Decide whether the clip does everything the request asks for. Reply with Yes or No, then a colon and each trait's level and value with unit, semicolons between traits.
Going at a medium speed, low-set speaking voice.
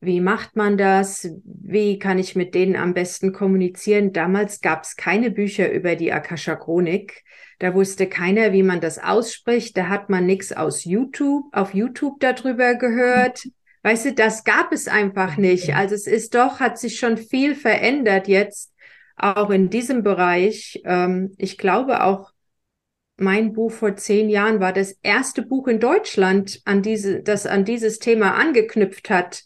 No: average, 165 wpm; high, 205 Hz